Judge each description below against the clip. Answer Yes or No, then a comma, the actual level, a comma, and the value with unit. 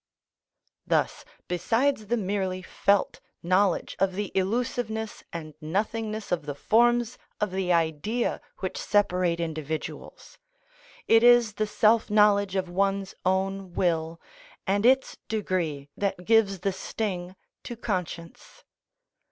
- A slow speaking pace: Yes, slow, 120 wpm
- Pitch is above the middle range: Yes, high, 195 Hz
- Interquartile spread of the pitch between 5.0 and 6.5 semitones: No, average, 3.6 semitones